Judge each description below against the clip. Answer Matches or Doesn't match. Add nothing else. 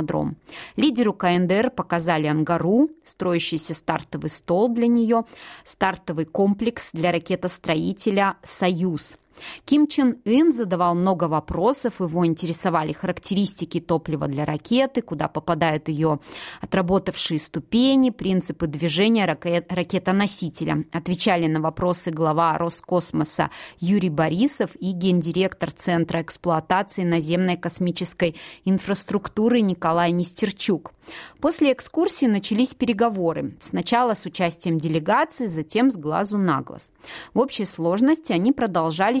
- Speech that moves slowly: Matches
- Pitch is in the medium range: Matches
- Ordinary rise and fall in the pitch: Matches